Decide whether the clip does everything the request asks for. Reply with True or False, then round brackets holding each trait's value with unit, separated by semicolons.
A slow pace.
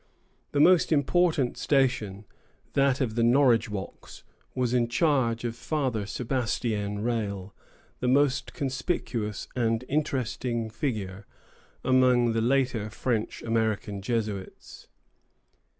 True (105 wpm)